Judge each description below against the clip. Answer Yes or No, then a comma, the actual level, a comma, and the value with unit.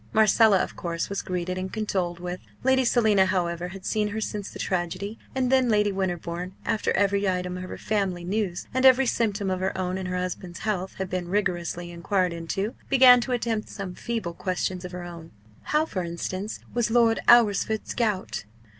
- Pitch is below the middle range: No, high, 190 Hz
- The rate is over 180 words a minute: Yes, average, 190 wpm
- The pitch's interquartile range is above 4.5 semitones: No, average, 3.4 semitones